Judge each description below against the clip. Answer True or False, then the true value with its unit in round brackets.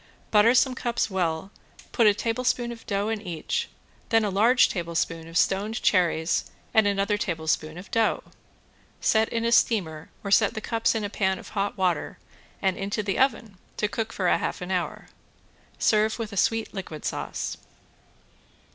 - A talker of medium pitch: False (205 Hz)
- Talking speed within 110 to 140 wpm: False (165 wpm)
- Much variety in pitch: False (3.6 semitones)